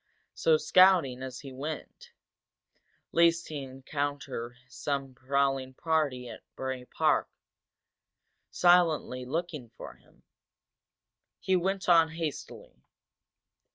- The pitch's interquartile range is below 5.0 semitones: Yes, average, 4.1 semitones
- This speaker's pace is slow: Yes, slow, 95 wpm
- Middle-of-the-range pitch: Yes, medium, 145 Hz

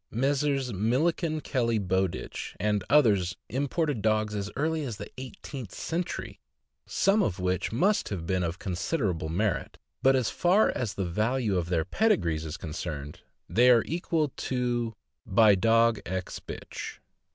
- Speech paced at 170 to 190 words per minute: No, average, 150 wpm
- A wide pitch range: Yes, wide, 6.5 semitones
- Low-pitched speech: Yes, low, 110 Hz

